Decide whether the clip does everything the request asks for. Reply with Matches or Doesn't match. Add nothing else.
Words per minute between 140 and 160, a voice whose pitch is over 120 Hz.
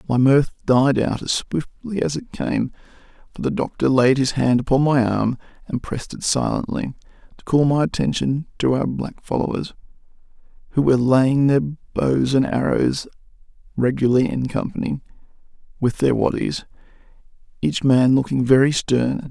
Matches